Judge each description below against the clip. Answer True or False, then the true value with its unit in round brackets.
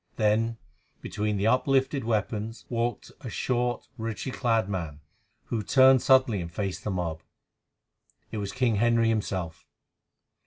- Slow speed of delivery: True (130 wpm)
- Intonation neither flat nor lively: True (3.2 semitones)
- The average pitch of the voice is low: True (110 Hz)